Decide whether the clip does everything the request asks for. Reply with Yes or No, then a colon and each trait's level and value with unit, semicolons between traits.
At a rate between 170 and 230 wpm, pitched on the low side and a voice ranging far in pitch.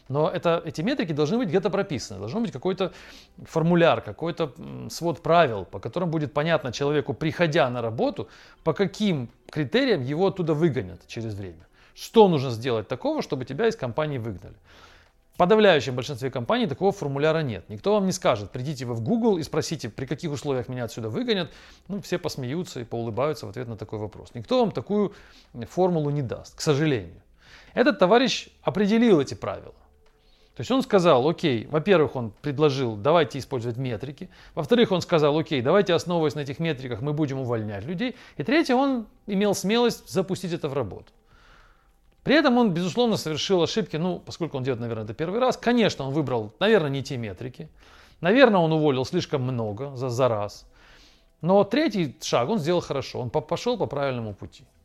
No: average, 175 wpm; medium, 155 Hz; wide, 6.5 semitones